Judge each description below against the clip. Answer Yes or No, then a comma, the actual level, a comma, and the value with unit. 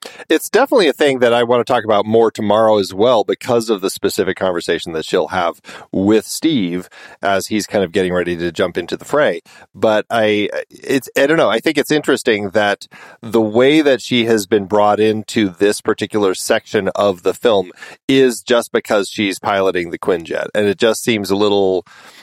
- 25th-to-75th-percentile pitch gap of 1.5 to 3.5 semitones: Yes, average, 2.9 semitones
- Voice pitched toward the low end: Yes, low, 110 Hz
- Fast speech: No, average, 195 wpm